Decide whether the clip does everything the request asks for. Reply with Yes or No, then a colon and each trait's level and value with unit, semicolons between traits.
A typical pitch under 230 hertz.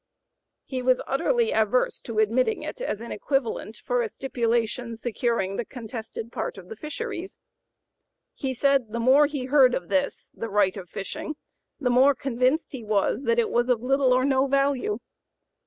No: high, 245 Hz